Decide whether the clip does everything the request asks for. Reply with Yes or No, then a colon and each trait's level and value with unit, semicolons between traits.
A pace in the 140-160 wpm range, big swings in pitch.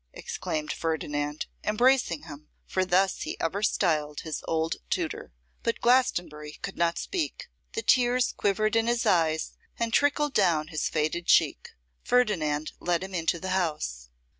Yes: average, 145 wpm; wide, 6.4 semitones